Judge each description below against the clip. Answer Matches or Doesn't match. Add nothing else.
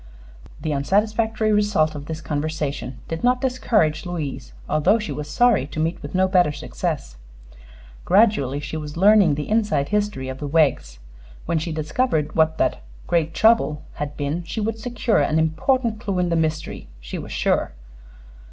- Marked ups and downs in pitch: Matches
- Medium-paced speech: Matches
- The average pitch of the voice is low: Doesn't match